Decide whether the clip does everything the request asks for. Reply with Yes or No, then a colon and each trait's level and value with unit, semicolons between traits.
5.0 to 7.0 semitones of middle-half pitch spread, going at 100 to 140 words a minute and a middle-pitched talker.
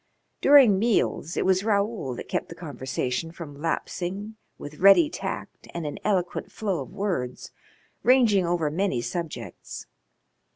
Yes: wide, 5.4 semitones; slow, 135 wpm; medium, 180 Hz